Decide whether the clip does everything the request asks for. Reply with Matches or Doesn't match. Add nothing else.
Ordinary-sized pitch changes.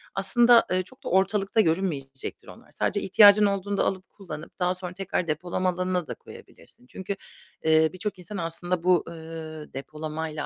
Matches